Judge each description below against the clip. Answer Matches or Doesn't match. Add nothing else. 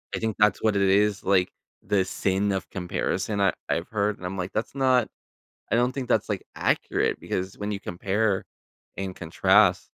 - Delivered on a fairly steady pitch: Matches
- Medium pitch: Doesn't match